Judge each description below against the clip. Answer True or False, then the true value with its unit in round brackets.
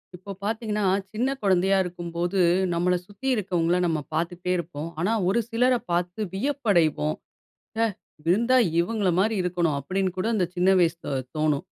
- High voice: False (180 Hz)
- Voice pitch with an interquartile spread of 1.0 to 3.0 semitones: False (3.5 semitones)